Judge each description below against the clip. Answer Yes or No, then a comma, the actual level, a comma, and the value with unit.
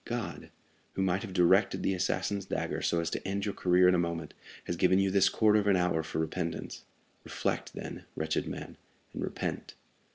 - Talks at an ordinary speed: Yes, average, 195 wpm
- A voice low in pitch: Yes, very low, 90 Hz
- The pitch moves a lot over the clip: No, narrow, 2.5 semitones